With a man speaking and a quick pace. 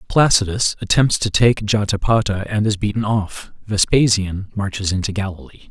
No: male; slow, 135 wpm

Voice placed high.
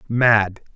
No: low, 110 Hz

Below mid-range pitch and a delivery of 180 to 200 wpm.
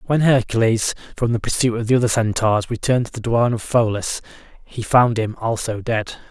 Yes: low, 115 Hz; average, 190 wpm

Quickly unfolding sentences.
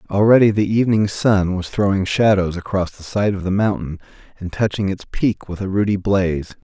No: average, 190 wpm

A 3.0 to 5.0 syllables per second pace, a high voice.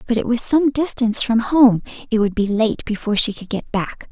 No: 5.5 syllables/s; high, 230 Hz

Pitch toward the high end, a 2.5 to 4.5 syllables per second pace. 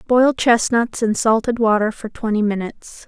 No: high, 225 Hz; 4.8 syllables/s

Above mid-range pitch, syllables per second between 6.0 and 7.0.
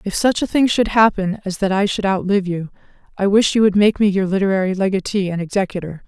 Yes: high, 195 Hz; 6.2 syllables/s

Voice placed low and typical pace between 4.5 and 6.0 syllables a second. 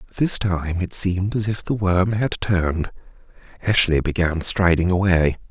Yes: very low, 95 Hz; 4.8 syllables/s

